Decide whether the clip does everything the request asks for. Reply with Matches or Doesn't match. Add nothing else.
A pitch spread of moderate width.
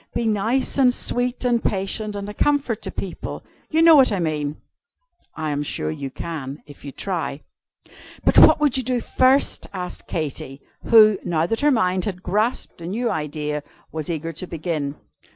Doesn't match